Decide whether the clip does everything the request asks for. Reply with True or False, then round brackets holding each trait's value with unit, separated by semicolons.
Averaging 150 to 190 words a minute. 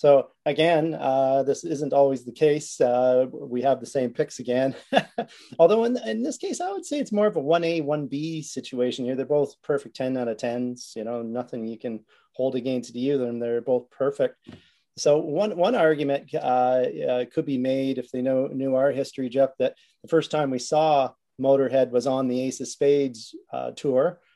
False (200 wpm)